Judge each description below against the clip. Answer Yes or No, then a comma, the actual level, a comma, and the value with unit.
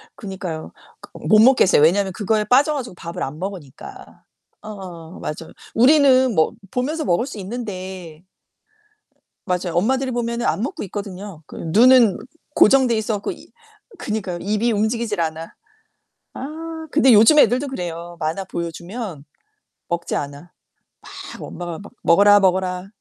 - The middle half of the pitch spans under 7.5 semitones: Yes, wide, 5.6 semitones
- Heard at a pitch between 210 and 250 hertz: No, high, 200 Hz